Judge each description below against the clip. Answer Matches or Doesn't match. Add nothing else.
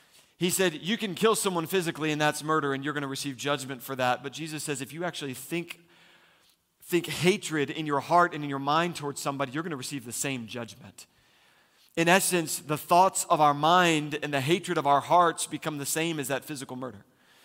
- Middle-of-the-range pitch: Matches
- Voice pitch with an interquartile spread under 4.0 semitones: Matches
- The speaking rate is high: Matches